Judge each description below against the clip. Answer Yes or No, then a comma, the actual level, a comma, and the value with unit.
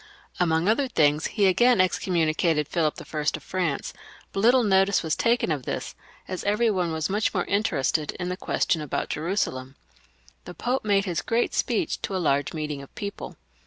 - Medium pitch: Yes, medium, 180 Hz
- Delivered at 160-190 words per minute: Yes, average, 185 wpm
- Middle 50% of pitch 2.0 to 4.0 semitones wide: No, average, 4.7 semitones